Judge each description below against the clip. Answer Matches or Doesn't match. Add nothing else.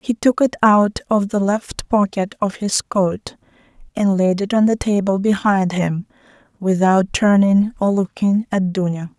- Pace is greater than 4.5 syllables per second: Doesn't match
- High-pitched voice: Matches